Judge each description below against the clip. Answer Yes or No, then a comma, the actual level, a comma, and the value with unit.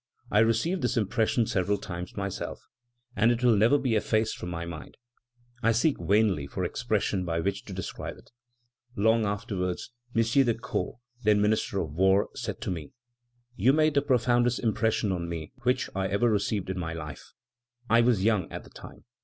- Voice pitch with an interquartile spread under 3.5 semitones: No, average, 3.9 semitones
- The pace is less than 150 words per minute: No, average, 180 wpm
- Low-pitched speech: Yes, low, 105 Hz